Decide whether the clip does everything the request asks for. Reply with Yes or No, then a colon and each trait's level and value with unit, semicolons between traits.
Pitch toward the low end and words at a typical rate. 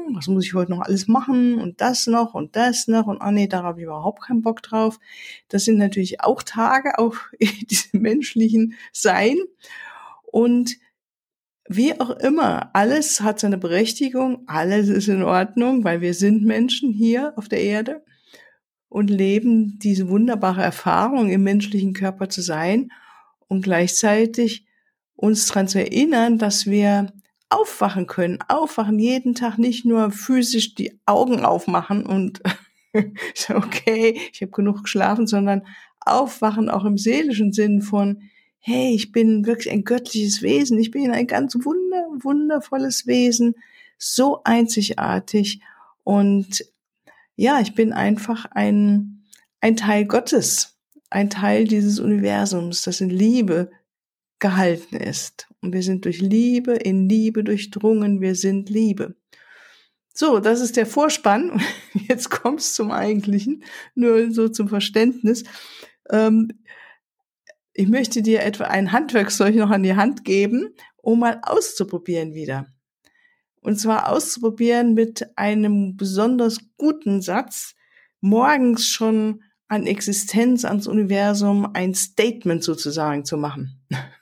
No: high, 220 Hz; average, 135 wpm